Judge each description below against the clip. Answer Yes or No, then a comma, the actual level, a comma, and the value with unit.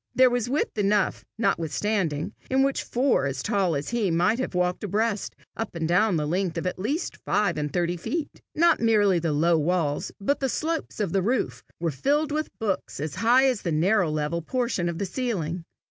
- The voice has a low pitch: No, high, 195 Hz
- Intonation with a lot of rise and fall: Yes, wide, 6.2 semitones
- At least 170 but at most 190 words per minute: No, average, 200 wpm